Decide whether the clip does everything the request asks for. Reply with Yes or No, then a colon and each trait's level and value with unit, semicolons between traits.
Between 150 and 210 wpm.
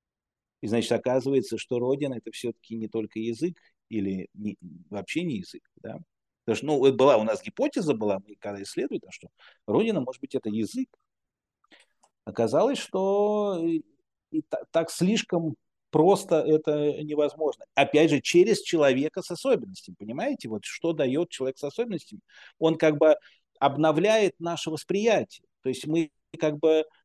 Yes: average, 155 wpm